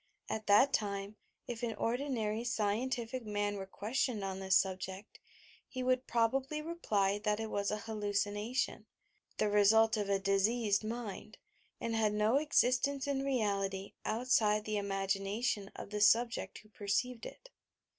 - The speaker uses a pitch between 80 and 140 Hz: No, high, 215 Hz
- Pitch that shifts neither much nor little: Yes, average, 3.2 semitones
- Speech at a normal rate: Yes, average, 145 wpm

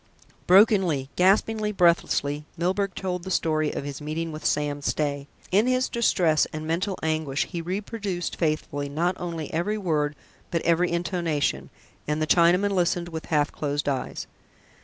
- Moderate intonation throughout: Yes, average, 3.6 semitones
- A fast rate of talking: No, average, 150 wpm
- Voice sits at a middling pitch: Yes, medium, 170 Hz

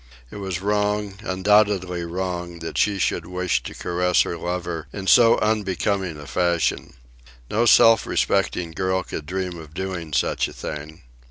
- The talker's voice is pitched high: No, very low, 90 Hz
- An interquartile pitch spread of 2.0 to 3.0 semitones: Yes, average, 2.7 semitones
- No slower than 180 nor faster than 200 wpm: No, average, 155 wpm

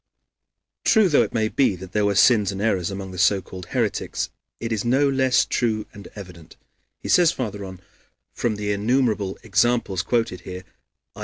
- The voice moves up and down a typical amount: Yes, average, 3.9 semitones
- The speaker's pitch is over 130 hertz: No, low, 105 Hz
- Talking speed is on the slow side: No, average, 180 wpm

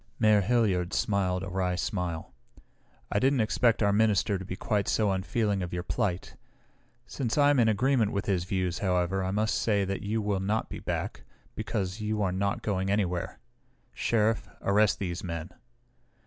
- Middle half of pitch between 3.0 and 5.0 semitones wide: No, narrow, 2.6 semitones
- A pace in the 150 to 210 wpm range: Yes, average, 175 wpm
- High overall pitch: No, low, 100 Hz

